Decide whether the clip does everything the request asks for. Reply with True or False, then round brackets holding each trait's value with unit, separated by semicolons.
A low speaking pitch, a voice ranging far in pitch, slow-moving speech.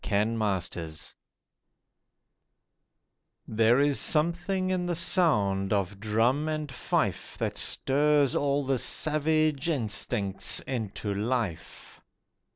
True (130 Hz; 6.7 semitones; 95 wpm)